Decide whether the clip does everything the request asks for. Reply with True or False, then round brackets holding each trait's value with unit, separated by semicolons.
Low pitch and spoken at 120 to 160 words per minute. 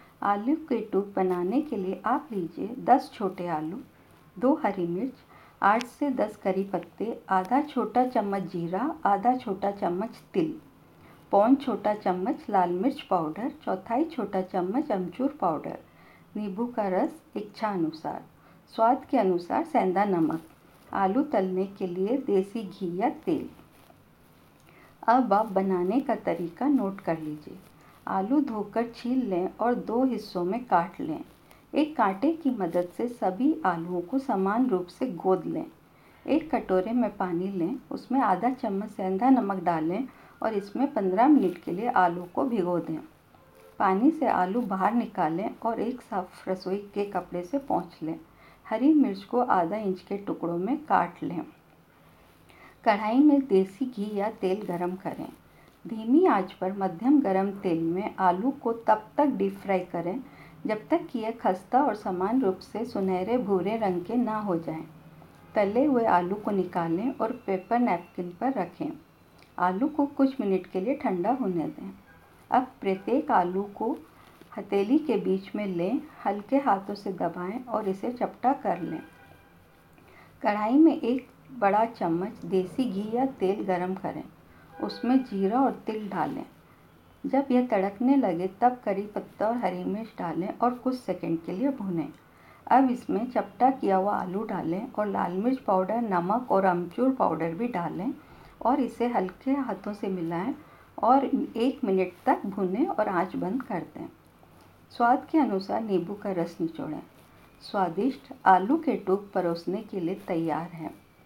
False (205 Hz; 155 wpm)